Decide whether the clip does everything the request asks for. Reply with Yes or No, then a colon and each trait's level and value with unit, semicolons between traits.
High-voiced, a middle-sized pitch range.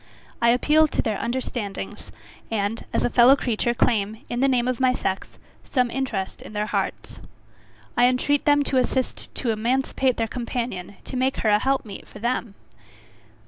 Yes: high, 240 Hz; average, 3.2 semitones